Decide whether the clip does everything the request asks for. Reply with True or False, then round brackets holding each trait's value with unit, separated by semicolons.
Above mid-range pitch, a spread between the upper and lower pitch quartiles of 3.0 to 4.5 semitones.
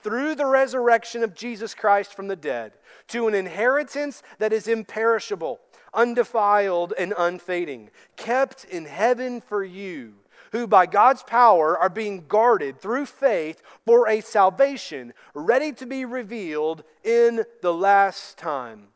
True (225 Hz; 3.8 semitones)